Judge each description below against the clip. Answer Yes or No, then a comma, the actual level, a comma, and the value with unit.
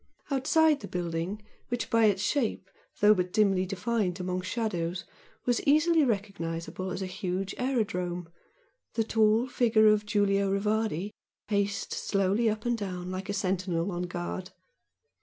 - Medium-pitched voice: No, high, 200 Hz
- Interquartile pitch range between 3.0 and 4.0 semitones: Yes, average, 3.3 semitones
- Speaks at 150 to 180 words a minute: No, average, 140 wpm